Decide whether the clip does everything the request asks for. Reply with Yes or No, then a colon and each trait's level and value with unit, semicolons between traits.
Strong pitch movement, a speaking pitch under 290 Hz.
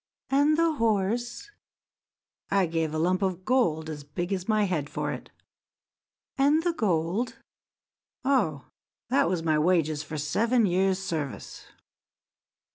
Yes: wide, 6.8 semitones; medium, 185 Hz